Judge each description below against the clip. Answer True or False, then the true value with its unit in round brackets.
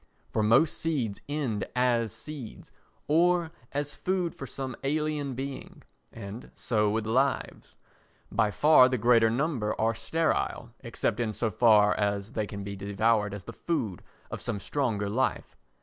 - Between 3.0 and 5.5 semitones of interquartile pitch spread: True (5.0 semitones)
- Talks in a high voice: False (115 Hz)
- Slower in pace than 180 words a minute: True (150 wpm)